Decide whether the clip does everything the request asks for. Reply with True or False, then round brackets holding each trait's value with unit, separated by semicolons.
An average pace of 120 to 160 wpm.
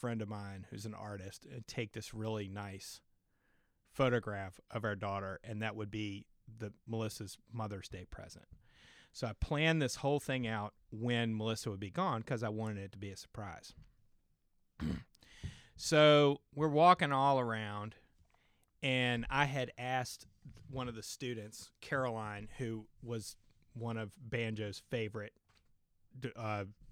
True (145 wpm)